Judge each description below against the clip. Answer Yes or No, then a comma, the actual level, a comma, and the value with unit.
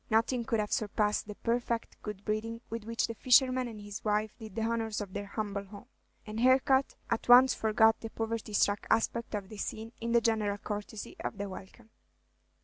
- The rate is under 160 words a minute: No, average, 195 wpm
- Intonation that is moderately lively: No, narrow, 1.9 semitones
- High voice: Yes, high, 220 Hz